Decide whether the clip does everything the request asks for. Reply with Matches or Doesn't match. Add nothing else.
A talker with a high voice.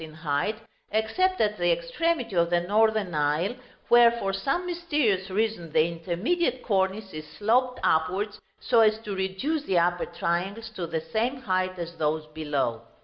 Matches